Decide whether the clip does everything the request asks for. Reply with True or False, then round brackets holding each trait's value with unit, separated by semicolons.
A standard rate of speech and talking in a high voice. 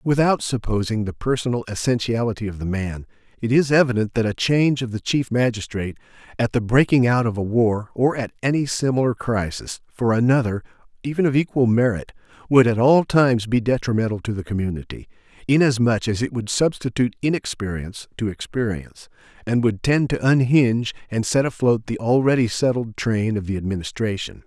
False (165 wpm; 120 Hz)